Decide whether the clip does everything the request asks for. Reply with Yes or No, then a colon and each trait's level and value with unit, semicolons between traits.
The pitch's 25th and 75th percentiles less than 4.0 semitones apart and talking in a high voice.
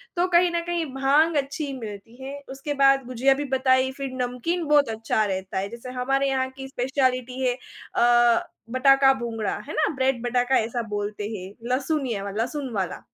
Yes: average, 2.7 semitones; very high, 260 Hz